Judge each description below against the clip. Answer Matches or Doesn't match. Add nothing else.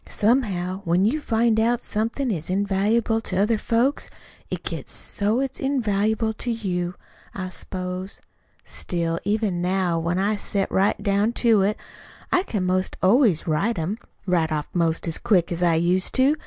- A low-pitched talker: Doesn't match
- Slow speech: Doesn't match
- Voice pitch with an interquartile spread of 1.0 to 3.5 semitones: Doesn't match